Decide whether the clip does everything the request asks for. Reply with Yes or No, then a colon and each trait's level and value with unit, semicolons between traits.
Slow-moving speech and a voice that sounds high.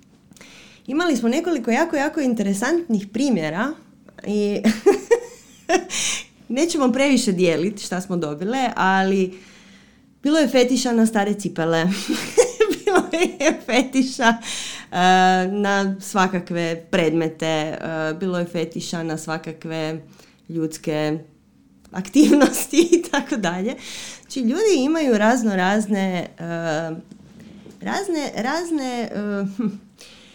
Yes: slow, 95 wpm; high, 210 Hz